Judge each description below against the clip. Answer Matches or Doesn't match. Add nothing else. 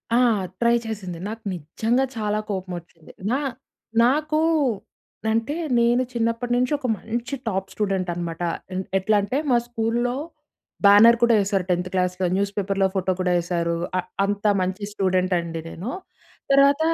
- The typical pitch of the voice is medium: Doesn't match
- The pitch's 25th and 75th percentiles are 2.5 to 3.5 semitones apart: Doesn't match